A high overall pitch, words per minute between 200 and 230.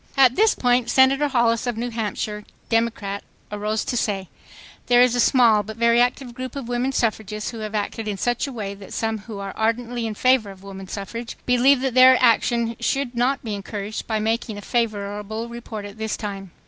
Yes: high, 230 Hz; fast, 205 wpm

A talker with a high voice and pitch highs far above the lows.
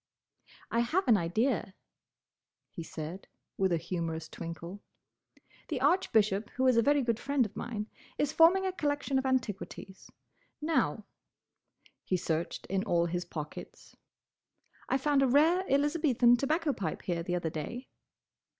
Yes: high, 230 Hz; wide, 8.0 semitones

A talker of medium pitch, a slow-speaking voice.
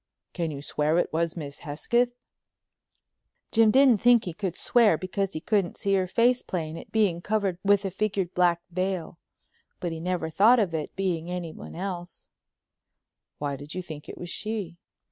No: medium, 180 Hz; average, 175 wpm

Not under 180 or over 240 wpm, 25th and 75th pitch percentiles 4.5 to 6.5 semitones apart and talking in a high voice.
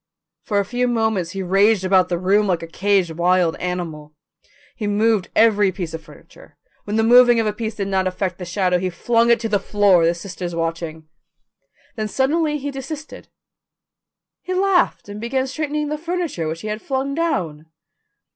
Yes: average, 185 wpm; wide, 5.4 semitones; high, 205 Hz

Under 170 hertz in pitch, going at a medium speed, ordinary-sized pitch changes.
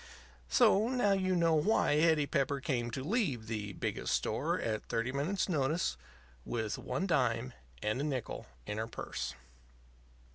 No: medium, 140 Hz; average, 150 wpm; wide, 6.8 semitones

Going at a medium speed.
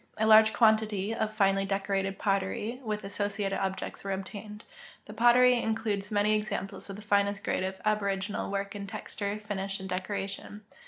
Yes: average, 160 wpm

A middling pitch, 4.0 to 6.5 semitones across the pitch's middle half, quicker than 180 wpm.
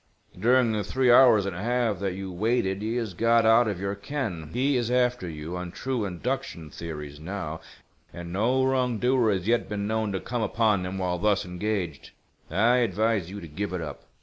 No: low, 105 Hz; average, 4.8 semitones; average, 200 wpm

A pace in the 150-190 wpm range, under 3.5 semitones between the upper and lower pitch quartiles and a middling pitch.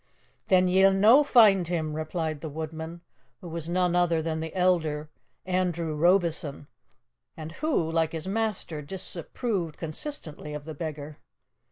No: average, 140 wpm; average, 2.8 semitones; medium, 165 Hz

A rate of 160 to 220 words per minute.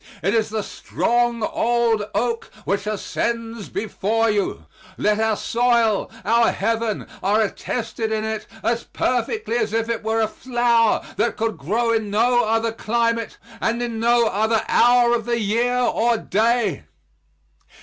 No: average, 150 wpm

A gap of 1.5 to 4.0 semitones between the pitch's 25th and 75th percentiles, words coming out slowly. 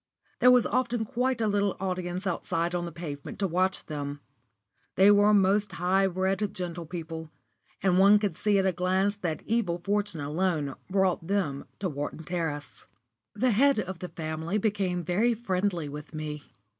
No: average, 3.6 semitones; average, 165 wpm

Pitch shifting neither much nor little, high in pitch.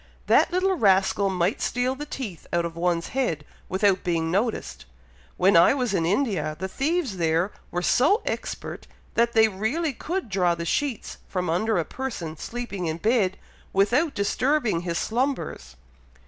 No: wide, 6.8 semitones; high, 200 Hz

